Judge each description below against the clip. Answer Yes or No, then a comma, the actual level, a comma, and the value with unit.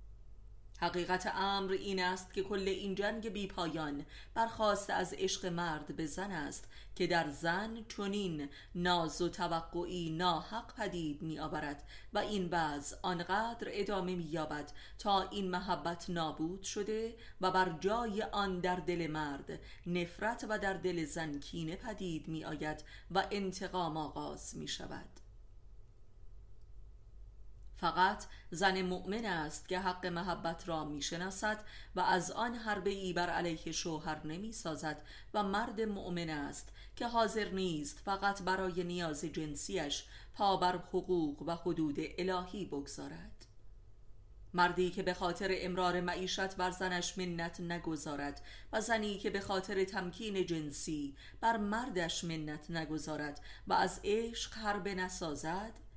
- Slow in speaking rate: No, average, 130 wpm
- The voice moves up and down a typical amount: Yes, average, 4.0 semitones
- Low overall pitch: No, medium, 175 Hz